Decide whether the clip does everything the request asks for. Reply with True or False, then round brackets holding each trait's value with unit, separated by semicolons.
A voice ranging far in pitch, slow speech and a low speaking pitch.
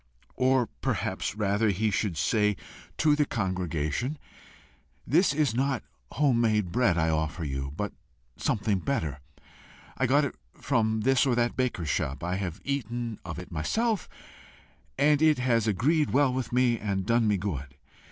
False (6.2 semitones; 155 wpm; 110 Hz)